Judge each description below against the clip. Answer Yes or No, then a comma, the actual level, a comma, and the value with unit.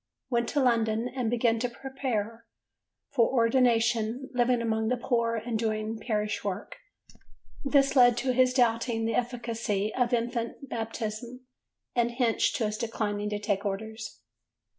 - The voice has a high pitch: Yes, high, 230 Hz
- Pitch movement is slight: Yes, narrow, 2.0 semitones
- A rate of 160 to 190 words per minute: No, average, 140 wpm